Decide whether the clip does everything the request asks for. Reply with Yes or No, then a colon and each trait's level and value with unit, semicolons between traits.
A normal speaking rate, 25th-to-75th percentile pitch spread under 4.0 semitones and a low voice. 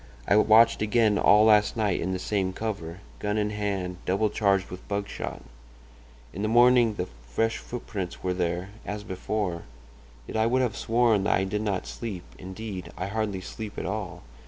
Yes: average, 175 wpm; average, 2.7 semitones; low, 105 Hz